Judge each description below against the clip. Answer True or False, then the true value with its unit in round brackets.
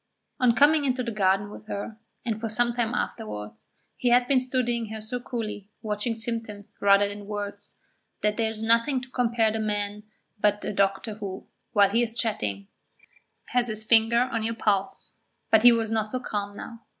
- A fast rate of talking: False (190 wpm)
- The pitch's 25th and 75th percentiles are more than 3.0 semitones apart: False (2.5 semitones)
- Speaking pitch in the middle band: False (220 Hz)